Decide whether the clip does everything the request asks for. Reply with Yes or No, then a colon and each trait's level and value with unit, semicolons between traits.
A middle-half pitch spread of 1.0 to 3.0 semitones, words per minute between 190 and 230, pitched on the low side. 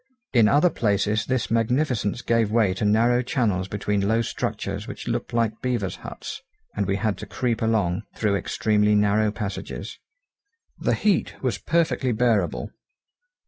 No: average, 2.7 semitones; average, 145 wpm; low, 110 Hz